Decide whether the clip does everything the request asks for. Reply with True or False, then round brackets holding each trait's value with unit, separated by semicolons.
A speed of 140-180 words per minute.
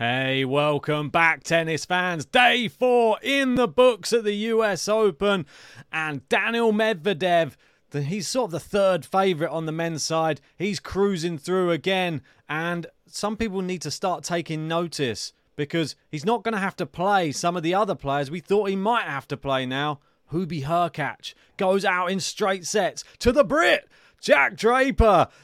True (175 wpm)